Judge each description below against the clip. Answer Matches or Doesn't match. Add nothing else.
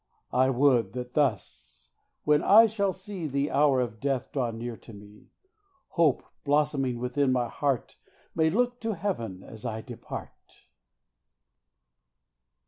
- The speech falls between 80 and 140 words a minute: Matches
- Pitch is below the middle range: Matches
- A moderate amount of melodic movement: Matches